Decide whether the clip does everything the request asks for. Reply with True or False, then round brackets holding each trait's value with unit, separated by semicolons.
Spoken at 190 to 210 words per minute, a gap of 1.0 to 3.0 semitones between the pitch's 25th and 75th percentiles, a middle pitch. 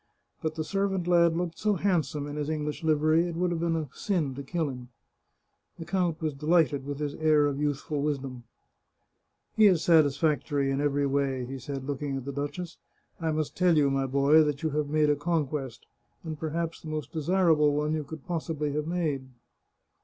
True (200 wpm; 2.6 semitones; 150 Hz)